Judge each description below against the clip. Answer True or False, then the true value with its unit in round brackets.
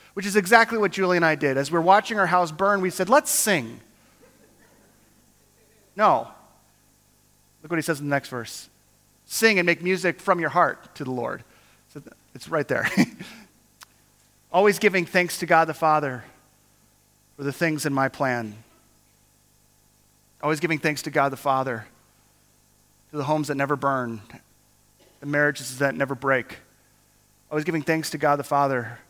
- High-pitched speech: False (140 Hz)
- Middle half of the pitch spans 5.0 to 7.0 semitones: True (5.5 semitones)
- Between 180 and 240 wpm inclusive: False (165 wpm)